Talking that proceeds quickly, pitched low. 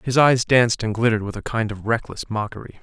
Yes: fast, 235 wpm; low, 115 Hz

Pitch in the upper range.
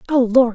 Yes: high, 245 Hz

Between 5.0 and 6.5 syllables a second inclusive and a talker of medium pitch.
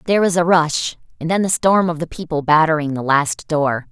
Yes: 5.4 syllables/s; medium, 160 Hz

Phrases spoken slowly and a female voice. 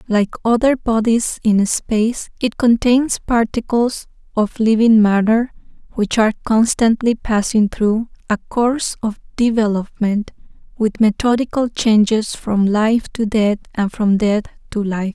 Yes: slow, 125 wpm; female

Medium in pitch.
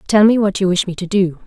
No: high, 195 Hz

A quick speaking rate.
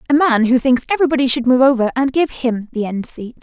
Yes: fast, 245 wpm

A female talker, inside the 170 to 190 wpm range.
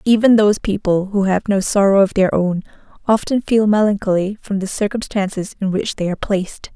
Yes: female; average, 185 wpm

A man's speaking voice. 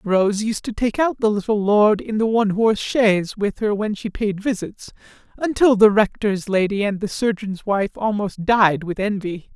Yes: male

